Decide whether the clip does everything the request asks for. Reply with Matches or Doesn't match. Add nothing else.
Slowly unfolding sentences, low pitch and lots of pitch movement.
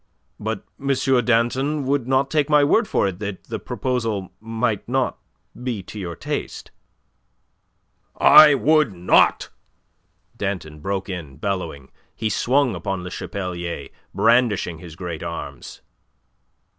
Matches